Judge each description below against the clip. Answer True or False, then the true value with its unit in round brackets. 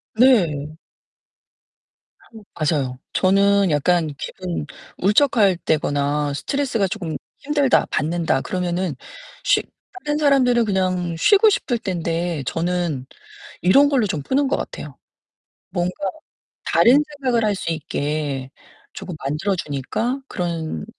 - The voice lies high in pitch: False (180 Hz)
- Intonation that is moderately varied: False (7.4 semitones)